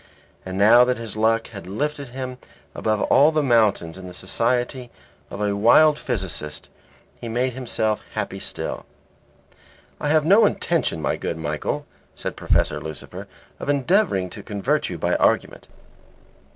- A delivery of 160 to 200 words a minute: No, average, 150 wpm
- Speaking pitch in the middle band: No, low, 115 Hz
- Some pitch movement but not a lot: No, wide, 6.1 semitones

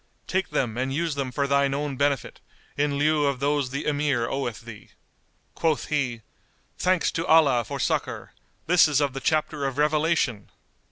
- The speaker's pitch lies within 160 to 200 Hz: No, medium, 140 Hz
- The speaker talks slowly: No, average, 170 wpm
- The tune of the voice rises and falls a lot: No, narrow, 2.4 semitones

